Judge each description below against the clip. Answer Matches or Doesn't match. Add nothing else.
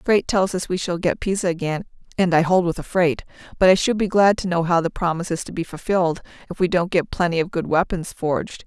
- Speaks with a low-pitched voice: Doesn't match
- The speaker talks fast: Matches